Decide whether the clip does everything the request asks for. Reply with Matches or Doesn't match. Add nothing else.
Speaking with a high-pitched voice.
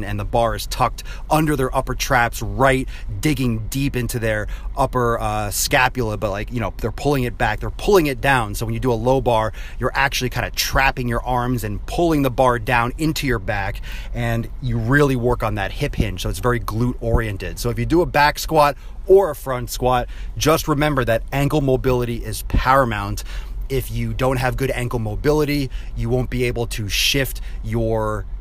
Doesn't match